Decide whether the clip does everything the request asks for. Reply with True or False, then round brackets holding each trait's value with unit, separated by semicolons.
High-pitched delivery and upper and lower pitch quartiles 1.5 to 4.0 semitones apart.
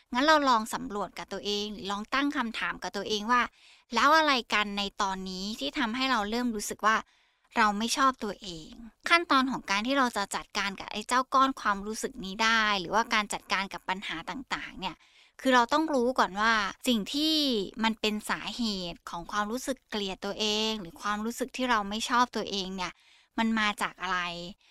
True (215 Hz; 3.6 semitones)